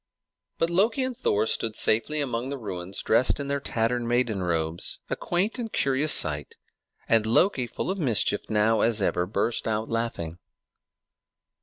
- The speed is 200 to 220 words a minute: No, average, 160 wpm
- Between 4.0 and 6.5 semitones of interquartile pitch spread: Yes, average, 5.1 semitones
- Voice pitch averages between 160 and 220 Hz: No, low, 115 Hz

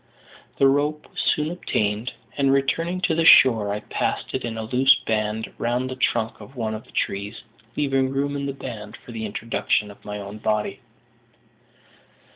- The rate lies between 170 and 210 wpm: Yes, average, 180 wpm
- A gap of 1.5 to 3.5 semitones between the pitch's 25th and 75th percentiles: No, average, 4.4 semitones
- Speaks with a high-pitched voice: No, low, 120 Hz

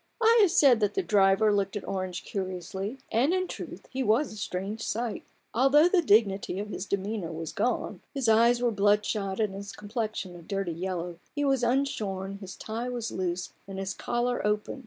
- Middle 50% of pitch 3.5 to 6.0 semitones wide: Yes, average, 4.0 semitones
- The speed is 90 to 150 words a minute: No, average, 190 wpm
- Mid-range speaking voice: No, high, 210 Hz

